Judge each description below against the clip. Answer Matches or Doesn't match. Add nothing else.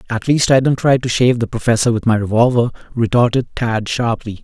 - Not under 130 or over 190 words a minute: Doesn't match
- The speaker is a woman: Doesn't match